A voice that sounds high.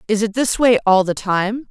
Yes: high, 215 Hz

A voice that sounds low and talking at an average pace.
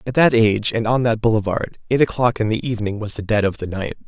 No: low, 110 Hz; fast, 265 wpm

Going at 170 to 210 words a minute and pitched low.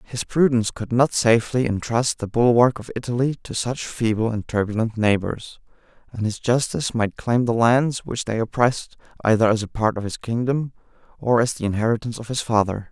Yes: average, 185 wpm; low, 115 Hz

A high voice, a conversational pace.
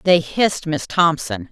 No: medium, 160 Hz; average, 160 wpm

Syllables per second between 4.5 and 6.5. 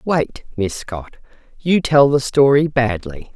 No: 3.7 syllables/s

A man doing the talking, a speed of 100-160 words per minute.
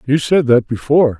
No: male; average, 200 wpm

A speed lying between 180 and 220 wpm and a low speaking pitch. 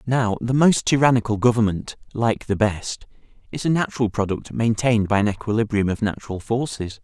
No: average, 160 wpm; low, 110 Hz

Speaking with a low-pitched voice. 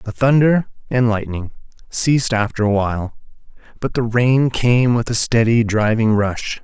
Yes: low, 115 Hz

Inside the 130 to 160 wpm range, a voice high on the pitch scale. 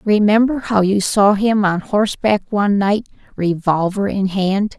Yes: average, 150 wpm; high, 200 Hz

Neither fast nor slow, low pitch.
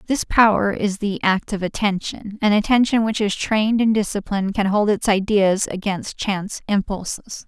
No: average, 170 wpm; high, 205 Hz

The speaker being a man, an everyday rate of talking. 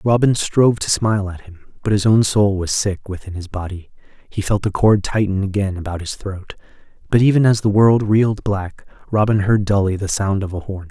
No: male; fast, 215 wpm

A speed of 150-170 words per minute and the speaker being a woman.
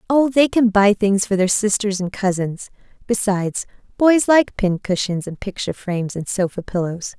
Yes: average, 165 wpm; female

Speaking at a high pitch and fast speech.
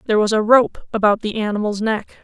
Yes: high, 215 Hz; fast, 215 wpm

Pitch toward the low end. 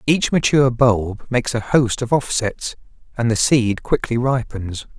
Yes: low, 120 Hz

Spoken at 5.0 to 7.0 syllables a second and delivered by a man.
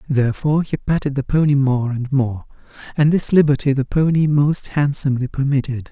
Yes: 5.5 syllables/s; male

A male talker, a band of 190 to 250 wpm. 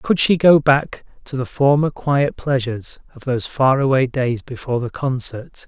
No: male; average, 170 wpm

